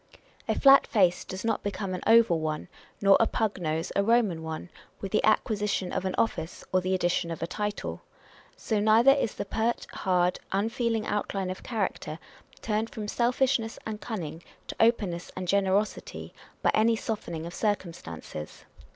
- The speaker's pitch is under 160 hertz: No, high, 200 Hz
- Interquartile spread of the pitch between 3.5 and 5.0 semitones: Yes, average, 3.8 semitones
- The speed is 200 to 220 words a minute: No, average, 170 wpm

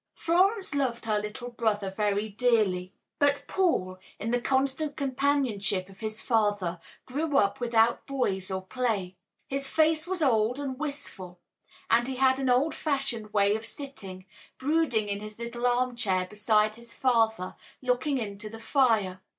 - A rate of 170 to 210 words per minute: No, average, 155 wpm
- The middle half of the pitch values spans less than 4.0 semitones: No, average, 4.7 semitones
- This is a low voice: No, high, 235 Hz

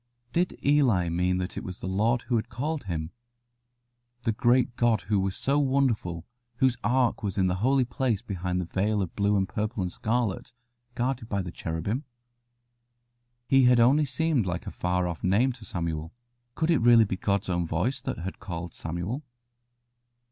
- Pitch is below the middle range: Yes, low, 105 Hz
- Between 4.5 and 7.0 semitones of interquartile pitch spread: Yes, wide, 5.6 semitones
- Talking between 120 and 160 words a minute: No, average, 175 wpm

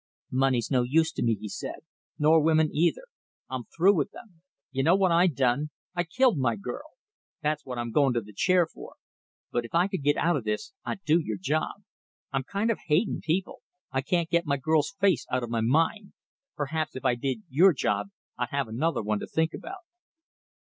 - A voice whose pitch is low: No, medium, 150 Hz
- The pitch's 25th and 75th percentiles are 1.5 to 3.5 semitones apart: No, average, 5.2 semitones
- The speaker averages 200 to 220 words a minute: Yes, fast, 205 wpm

